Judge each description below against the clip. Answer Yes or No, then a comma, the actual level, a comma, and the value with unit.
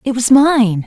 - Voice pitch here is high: Yes, high, 245 Hz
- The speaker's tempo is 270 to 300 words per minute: No, fast, 210 wpm